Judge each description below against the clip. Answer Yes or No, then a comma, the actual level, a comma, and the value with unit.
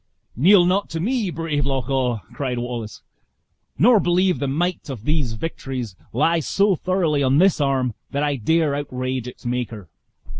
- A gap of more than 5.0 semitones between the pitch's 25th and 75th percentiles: Yes, wide, 5.5 semitones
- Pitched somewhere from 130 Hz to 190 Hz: Yes, medium, 140 Hz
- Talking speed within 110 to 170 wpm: Yes, average, 160 wpm